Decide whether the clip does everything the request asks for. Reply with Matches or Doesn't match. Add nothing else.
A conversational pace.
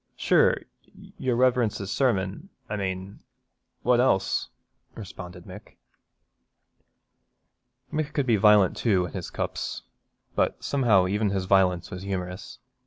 Doesn't match